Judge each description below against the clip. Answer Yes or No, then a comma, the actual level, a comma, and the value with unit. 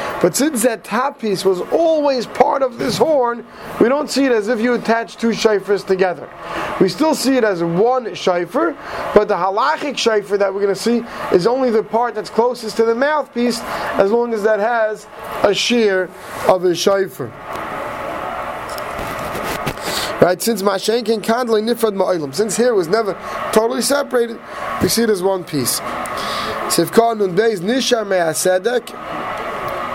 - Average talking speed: Yes, average, 160 wpm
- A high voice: Yes, high, 220 Hz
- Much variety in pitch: No, average, 3.7 semitones